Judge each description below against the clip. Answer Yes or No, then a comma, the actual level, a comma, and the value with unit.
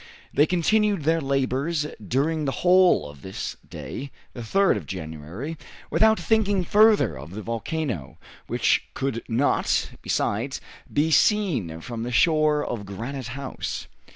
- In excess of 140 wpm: No, slow, 135 wpm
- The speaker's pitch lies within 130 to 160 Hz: Yes, medium, 140 Hz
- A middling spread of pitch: No, wide, 6.7 semitones